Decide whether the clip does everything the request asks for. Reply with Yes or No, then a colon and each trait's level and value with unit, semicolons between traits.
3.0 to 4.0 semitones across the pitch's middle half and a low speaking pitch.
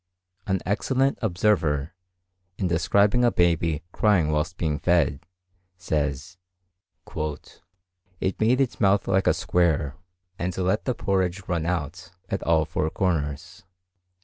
Yes: average, 3.7 semitones; very low, 90 Hz